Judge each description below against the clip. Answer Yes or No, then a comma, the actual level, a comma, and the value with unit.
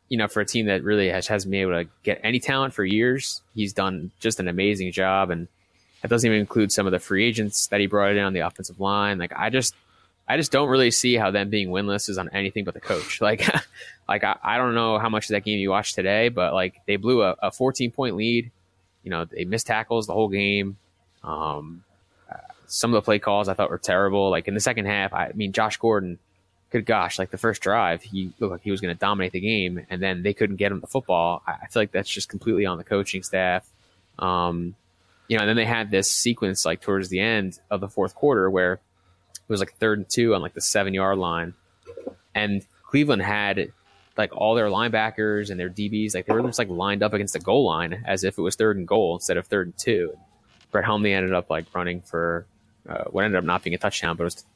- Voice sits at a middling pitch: No, low, 100 Hz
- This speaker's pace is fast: Yes, fast, 245 wpm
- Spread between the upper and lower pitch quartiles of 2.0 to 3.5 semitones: Yes, narrow, 2.6 semitones